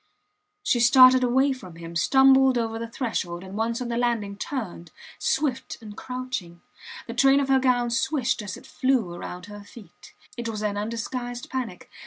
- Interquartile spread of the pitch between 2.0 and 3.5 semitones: No, average, 4.0 semitones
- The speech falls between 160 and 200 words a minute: Yes, average, 175 wpm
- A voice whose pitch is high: Yes, high, 235 Hz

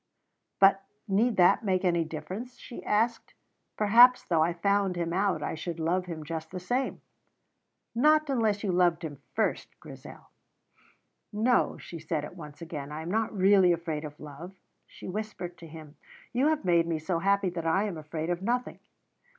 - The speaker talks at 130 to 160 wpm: No, average, 175 wpm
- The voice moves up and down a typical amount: Yes, average, 4.1 semitones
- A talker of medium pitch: Yes, medium, 180 Hz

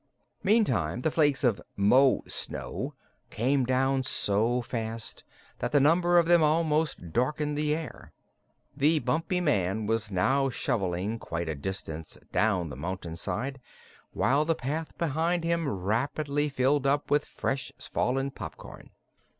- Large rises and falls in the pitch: Yes, wide, 6.1 semitones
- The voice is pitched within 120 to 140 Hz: Yes, low, 135 Hz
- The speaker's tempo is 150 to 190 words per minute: No, slow, 135 wpm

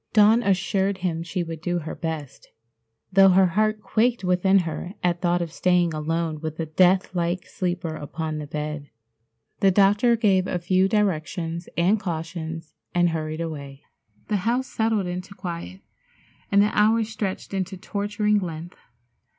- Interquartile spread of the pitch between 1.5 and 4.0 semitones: Yes, average, 3.5 semitones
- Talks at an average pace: Yes, average, 155 wpm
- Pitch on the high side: No, medium, 180 Hz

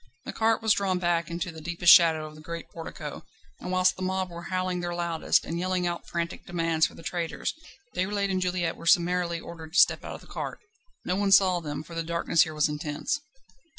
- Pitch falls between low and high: Yes, medium, 175 Hz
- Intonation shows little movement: Yes, narrow, 1.8 semitones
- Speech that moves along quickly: Yes, fast, 220 wpm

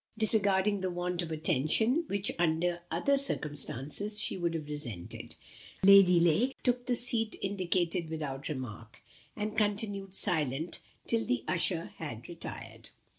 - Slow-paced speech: Yes, slow, 130 wpm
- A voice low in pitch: No, medium, 175 Hz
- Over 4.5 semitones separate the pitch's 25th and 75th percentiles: Yes, average, 5.2 semitones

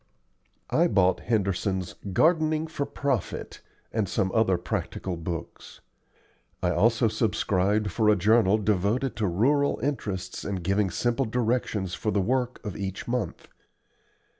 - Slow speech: Yes, slow, 130 wpm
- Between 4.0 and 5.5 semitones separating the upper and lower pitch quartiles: Yes, average, 4.4 semitones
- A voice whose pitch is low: Yes, low, 105 Hz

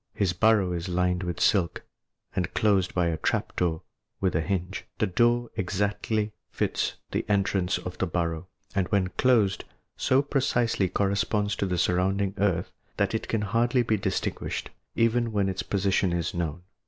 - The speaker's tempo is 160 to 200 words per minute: Yes, average, 165 wpm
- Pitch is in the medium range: No, very low, 95 Hz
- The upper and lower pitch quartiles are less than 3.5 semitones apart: Yes, average, 3.0 semitones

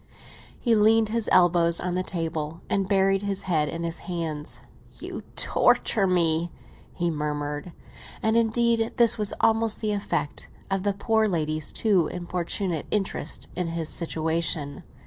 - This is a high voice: No, medium, 180 Hz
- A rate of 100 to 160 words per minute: Yes, average, 145 wpm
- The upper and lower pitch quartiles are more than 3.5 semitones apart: Yes, average, 4.3 semitones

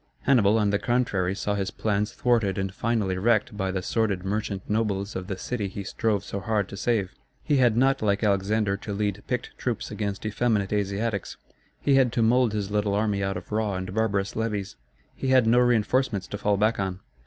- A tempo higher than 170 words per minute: Yes, average, 200 wpm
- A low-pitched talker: Yes, low, 105 Hz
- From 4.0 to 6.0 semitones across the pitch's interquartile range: No, narrow, 2.4 semitones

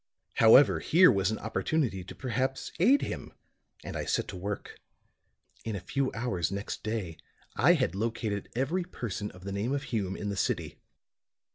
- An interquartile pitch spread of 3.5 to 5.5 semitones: Yes, average, 5.1 semitones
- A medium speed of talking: Yes, average, 170 wpm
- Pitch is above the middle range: No, low, 110 Hz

